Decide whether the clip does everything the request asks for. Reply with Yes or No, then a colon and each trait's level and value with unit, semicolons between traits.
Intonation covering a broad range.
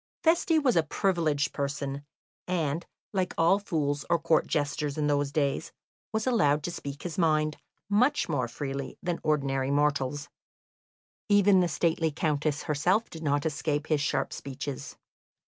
No: average, 3.4 semitones